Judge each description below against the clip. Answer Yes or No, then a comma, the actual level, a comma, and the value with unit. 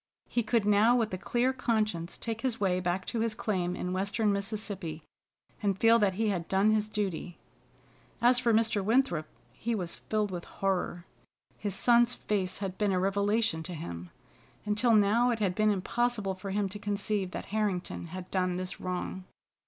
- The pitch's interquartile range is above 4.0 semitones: No, average, 3.2 semitones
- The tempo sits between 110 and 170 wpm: No, average, 180 wpm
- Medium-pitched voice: No, high, 205 Hz